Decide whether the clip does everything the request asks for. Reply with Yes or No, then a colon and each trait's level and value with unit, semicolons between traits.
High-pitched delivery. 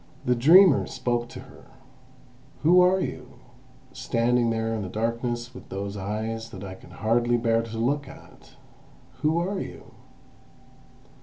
No: low, 120 Hz